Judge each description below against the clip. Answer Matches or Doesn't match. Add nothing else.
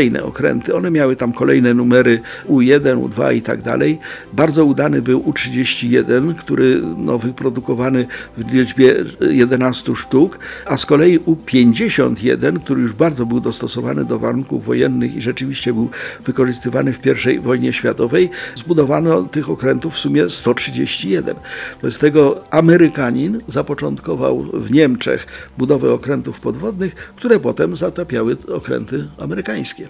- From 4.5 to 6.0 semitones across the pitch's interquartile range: Doesn't match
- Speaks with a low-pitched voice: Matches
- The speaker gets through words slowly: Doesn't match